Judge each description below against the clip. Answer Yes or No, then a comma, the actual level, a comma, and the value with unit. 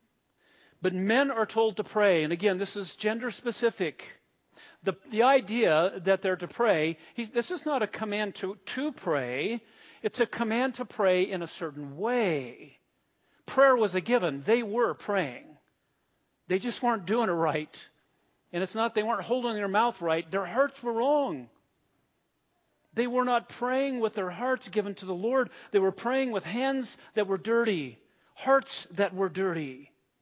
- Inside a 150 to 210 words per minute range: Yes, average, 170 wpm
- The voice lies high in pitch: Yes, high, 215 Hz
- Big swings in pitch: No, average, 4.1 semitones